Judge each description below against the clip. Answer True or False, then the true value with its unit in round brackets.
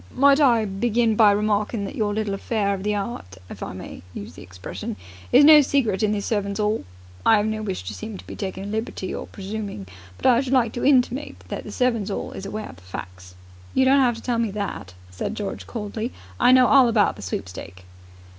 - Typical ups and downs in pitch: True (3.4 semitones)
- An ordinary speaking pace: False (225 wpm)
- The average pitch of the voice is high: True (215 Hz)